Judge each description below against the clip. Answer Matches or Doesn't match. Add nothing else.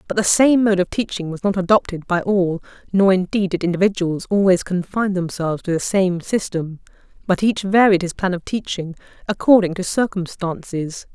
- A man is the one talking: Doesn't match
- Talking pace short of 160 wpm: Doesn't match